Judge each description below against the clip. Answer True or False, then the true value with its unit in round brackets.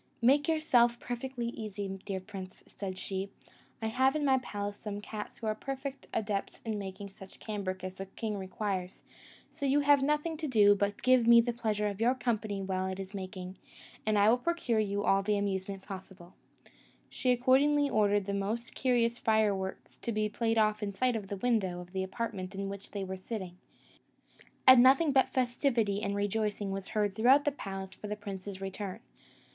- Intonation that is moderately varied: True (3.8 semitones)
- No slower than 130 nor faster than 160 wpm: False (195 wpm)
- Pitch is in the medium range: False (210 Hz)